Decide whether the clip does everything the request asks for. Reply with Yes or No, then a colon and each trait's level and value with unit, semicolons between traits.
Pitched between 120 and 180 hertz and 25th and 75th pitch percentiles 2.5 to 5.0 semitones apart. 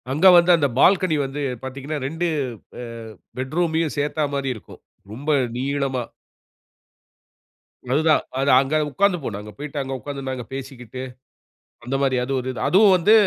Yes: medium, 140 Hz; average, 3.3 semitones